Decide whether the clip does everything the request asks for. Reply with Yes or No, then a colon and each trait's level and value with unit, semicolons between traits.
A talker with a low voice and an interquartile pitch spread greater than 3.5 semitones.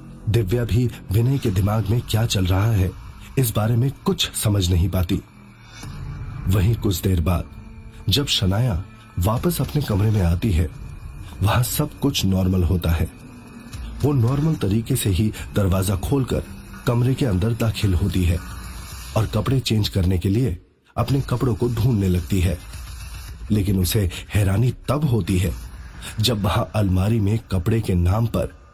Yes: low, 105 Hz; average, 4.0 semitones